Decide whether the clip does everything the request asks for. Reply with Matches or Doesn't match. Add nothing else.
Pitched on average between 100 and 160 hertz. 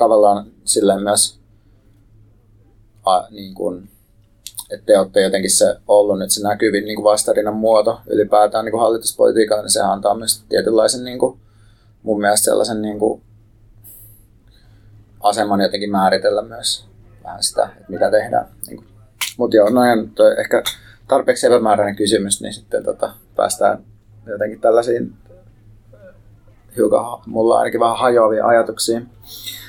Matches